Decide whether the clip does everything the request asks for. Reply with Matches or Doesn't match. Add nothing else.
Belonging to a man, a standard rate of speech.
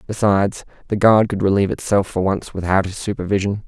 Matches